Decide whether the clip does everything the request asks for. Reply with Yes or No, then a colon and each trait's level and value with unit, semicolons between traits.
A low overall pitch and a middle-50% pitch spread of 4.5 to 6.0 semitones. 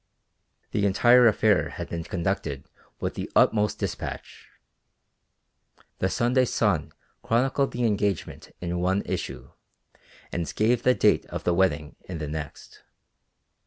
Yes: low, 100 Hz; average, 5.3 semitones